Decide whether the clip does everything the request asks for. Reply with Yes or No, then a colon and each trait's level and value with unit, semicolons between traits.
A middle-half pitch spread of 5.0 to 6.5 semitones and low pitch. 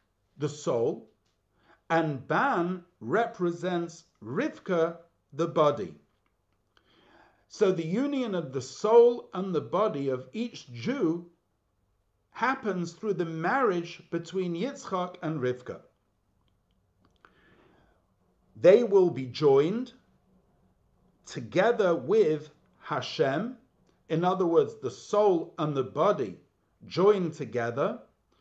No: average, 5.3 semitones; medium, 170 Hz